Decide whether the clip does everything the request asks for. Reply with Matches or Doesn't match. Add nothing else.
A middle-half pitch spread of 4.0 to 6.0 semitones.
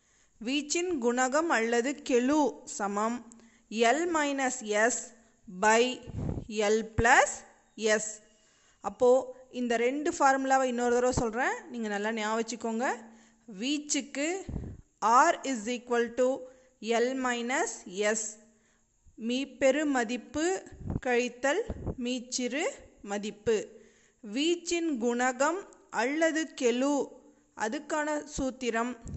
Doesn't match